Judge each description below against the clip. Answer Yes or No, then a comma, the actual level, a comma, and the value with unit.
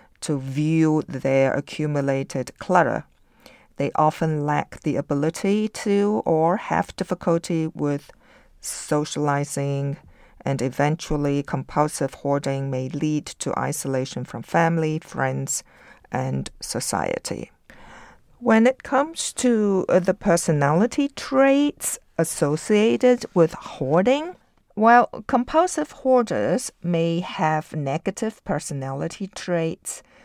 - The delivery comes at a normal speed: No, slow, 95 wpm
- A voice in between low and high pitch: Yes, medium, 160 Hz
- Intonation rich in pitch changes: Yes, wide, 6.1 semitones